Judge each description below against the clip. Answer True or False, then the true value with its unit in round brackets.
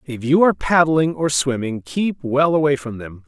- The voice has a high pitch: False (140 Hz)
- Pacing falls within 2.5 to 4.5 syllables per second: False (4.8 syllables/s)